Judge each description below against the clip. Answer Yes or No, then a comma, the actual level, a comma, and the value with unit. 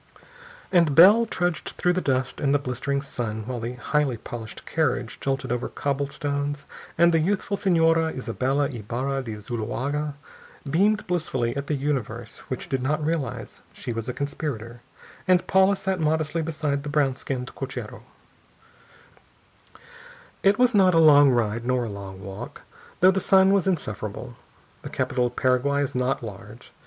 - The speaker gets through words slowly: No, average, 160 wpm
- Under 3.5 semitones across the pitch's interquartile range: No, average, 4.9 semitones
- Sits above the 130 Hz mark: Yes, medium, 140 Hz